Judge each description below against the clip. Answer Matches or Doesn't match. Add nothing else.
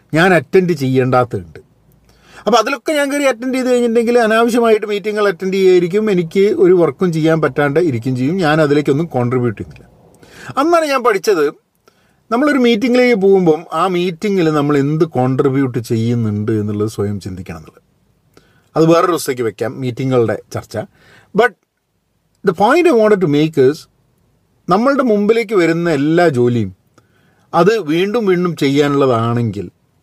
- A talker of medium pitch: Matches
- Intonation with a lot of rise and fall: Matches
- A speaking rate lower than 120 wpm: Doesn't match